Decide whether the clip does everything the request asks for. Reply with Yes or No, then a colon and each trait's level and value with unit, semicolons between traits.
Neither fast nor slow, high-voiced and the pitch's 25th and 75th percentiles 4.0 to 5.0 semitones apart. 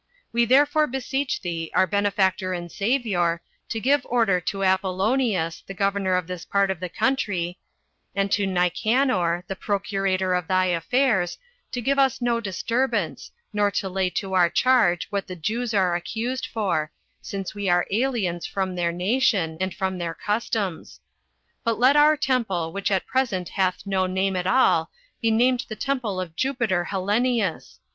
Yes: average, 165 wpm; high, 195 Hz; average, 4.6 semitones